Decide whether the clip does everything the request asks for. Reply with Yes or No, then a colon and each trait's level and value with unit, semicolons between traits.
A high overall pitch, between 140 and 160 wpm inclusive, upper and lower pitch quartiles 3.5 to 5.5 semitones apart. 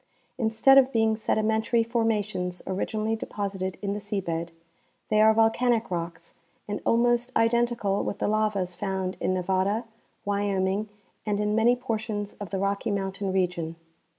No: high, 205 Hz; average, 145 wpm; narrow, 2.6 semitones